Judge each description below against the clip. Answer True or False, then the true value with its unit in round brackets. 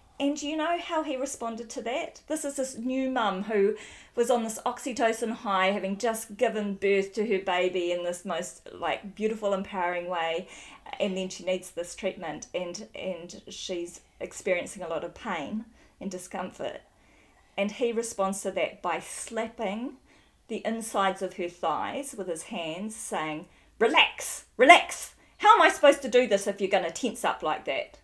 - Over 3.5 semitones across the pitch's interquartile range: True (4.8 semitones)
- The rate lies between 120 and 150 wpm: False (175 wpm)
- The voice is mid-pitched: False (210 Hz)